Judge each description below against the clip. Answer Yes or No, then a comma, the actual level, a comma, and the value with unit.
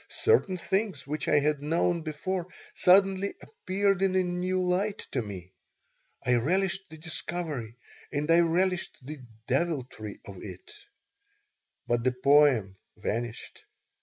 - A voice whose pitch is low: No, medium, 160 Hz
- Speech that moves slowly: Yes, slow, 130 wpm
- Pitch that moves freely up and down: Yes, wide, 6.7 semitones